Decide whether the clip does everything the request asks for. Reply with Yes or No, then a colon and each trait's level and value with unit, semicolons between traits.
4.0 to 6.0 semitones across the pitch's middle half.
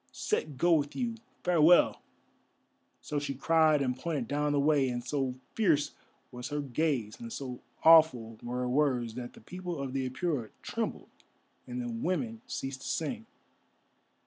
Yes: average, 4.4 semitones